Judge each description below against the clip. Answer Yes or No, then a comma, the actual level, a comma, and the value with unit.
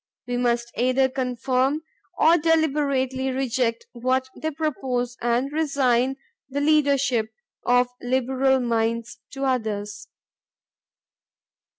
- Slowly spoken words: Yes, slow, 95 wpm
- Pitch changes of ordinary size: No, narrow, 2.3 semitones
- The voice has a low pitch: No, very high, 260 Hz